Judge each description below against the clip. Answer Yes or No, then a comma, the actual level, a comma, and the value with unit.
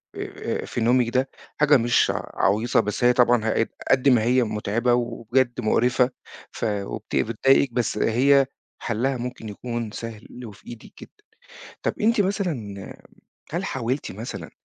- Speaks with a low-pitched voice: Yes, low, 120 Hz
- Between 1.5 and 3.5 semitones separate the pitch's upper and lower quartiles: Yes, narrow, 2.6 semitones